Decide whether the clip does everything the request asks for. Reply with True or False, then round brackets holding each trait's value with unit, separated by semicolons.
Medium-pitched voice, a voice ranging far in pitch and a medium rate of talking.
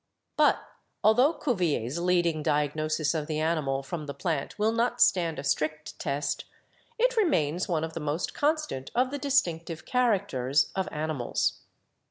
True (165 Hz; 6.6 semitones; 150 wpm)